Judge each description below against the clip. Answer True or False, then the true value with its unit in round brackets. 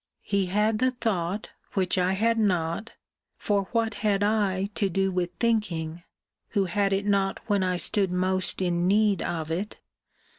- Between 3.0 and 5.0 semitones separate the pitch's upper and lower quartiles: False (2.5 semitones)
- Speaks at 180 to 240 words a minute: False (160 wpm)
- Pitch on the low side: False (195 Hz)